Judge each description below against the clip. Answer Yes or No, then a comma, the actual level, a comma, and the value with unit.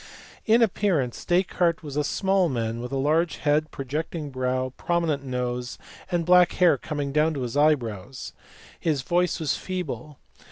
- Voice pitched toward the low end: No, medium, 150 Hz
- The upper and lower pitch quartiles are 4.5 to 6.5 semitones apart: Yes, average, 4.9 semitones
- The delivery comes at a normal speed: Yes, average, 150 wpm